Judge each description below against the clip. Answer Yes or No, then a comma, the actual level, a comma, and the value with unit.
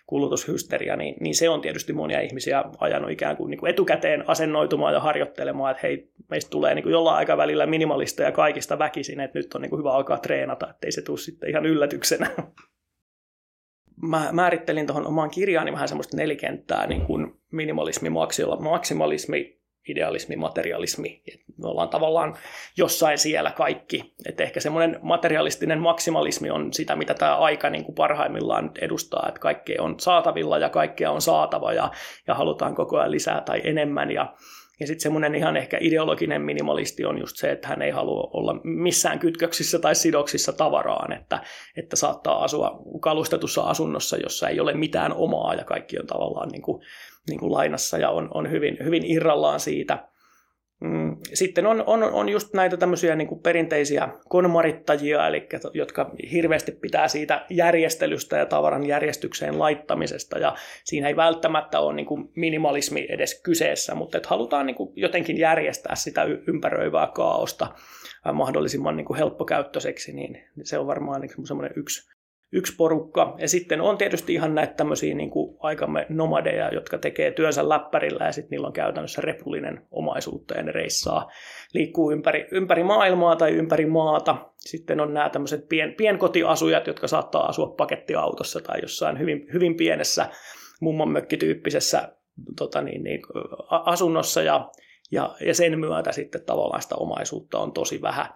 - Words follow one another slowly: No, fast, 155 wpm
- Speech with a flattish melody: Yes, narrow, 2.2 semitones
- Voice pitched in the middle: Yes, medium, 160 Hz